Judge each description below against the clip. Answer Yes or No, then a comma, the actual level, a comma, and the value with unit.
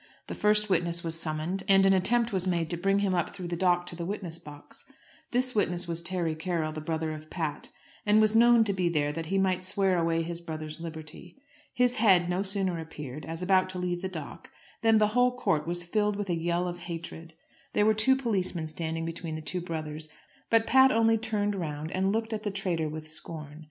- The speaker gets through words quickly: Yes, fast, 220 wpm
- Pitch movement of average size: Yes, average, 3.8 semitones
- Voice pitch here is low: No, medium, 175 Hz